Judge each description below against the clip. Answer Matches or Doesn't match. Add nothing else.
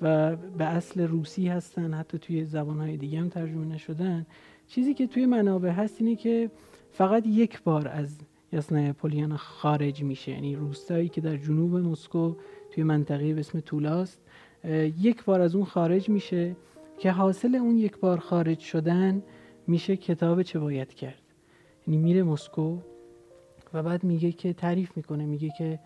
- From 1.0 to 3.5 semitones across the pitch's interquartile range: Matches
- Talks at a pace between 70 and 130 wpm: Doesn't match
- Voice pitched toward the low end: Doesn't match